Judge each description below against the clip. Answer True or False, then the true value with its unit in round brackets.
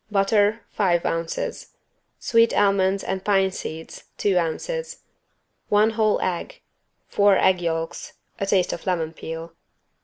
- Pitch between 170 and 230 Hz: True (190 Hz)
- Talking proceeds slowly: True (125 wpm)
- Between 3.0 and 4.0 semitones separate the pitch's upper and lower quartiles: True (3.4 semitones)